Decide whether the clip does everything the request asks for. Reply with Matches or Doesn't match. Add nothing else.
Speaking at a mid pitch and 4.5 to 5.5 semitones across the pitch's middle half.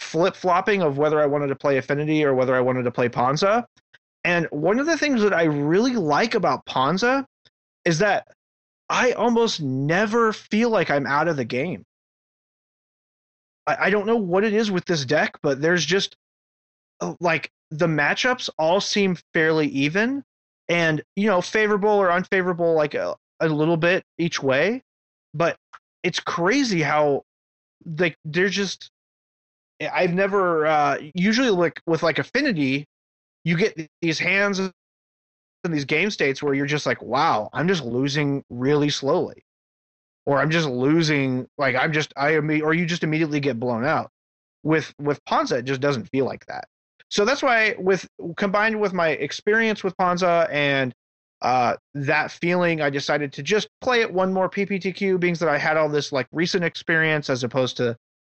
Matches